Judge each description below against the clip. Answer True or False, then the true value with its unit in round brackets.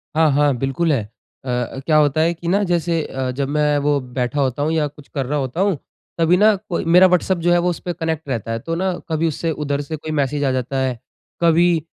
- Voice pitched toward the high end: False (150 Hz)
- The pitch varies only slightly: False (3.5 semitones)